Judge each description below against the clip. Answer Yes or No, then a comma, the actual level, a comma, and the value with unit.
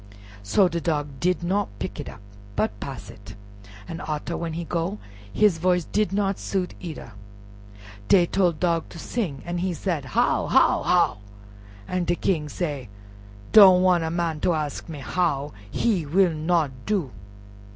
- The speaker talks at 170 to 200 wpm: No, average, 160 wpm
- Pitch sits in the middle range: Yes, medium, 170 Hz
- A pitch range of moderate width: Yes, average, 3.5 semitones